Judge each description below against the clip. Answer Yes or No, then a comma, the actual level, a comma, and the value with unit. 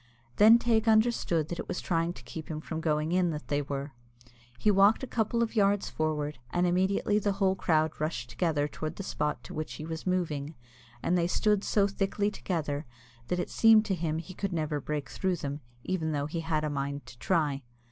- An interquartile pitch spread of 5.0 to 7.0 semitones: No, average, 4.4 semitones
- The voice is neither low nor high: Yes, medium, 165 Hz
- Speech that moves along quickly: Yes, fast, 215 wpm